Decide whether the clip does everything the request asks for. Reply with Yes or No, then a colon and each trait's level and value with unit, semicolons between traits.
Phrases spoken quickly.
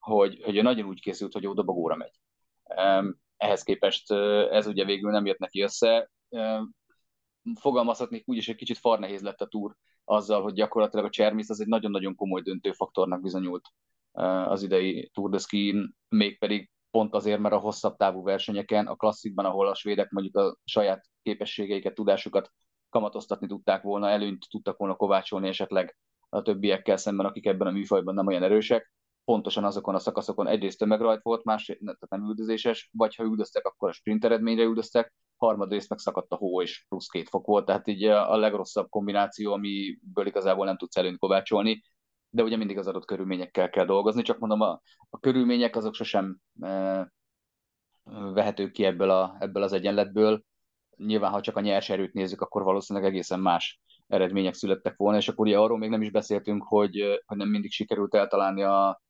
Yes: fast, 175 wpm